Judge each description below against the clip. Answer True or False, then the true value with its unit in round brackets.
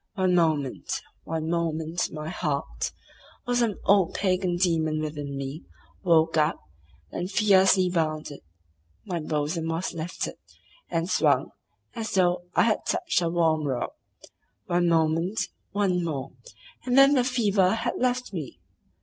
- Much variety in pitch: False (3.5 semitones)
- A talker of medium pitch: True (170 Hz)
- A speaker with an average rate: False (130 wpm)